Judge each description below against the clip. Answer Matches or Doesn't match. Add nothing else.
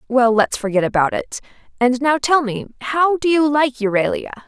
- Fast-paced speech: Doesn't match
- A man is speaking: Doesn't match